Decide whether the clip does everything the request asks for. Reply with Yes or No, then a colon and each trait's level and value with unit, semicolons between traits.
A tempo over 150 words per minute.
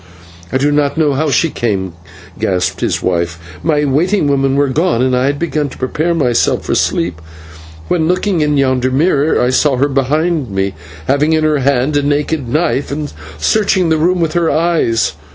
Yes: average, 190 wpm